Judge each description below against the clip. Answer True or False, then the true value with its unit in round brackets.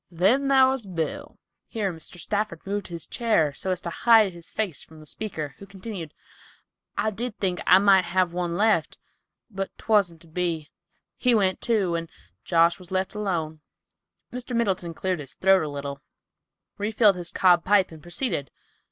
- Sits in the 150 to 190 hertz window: True (185 Hz)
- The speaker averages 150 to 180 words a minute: True (170 wpm)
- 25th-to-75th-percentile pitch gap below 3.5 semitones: False (4.0 semitones)